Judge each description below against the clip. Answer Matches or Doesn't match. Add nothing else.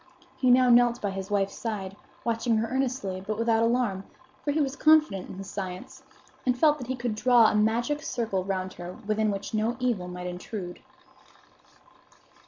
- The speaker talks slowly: Doesn't match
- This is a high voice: Matches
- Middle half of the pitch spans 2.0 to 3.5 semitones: Doesn't match